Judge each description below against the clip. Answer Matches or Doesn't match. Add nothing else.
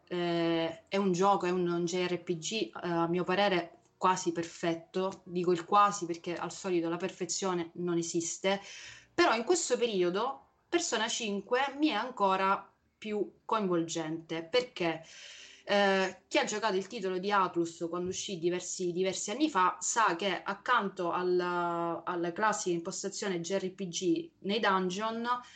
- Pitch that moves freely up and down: Doesn't match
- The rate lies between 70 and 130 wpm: Doesn't match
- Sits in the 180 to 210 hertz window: Matches